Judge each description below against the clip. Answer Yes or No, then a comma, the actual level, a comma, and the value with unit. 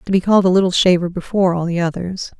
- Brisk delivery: Yes, fast, 250 wpm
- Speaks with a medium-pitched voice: Yes, medium, 180 Hz